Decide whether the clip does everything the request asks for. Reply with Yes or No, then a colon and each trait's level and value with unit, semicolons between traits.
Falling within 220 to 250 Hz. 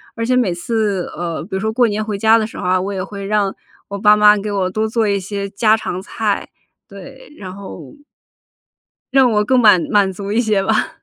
No: high, 205 Hz